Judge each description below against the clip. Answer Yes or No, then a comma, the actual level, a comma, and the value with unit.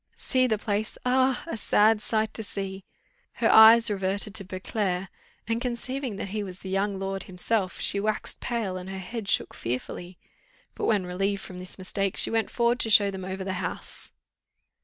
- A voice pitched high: Yes, high, 200 Hz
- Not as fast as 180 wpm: No, average, 185 wpm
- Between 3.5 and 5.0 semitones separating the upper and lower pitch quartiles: No, average, 2.8 semitones